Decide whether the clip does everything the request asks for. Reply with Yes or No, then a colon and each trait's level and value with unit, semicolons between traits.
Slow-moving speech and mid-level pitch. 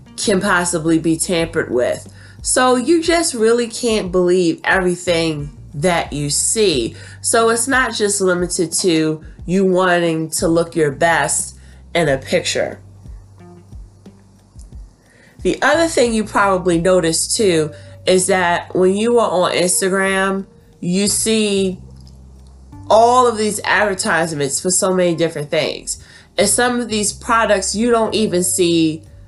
Yes: slow, 130 wpm; medium, 180 Hz